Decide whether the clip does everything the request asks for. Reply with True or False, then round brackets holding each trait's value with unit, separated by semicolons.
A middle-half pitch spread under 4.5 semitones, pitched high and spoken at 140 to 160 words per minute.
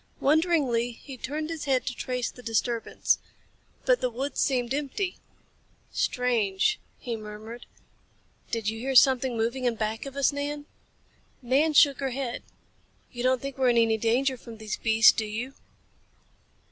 True (3.2 semitones; 250 Hz; 155 wpm)